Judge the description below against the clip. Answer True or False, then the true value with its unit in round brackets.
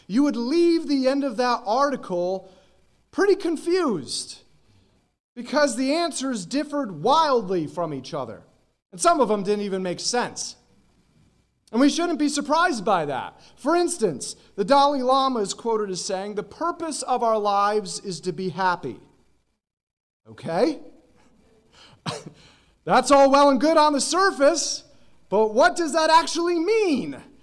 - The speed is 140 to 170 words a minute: True (145 wpm)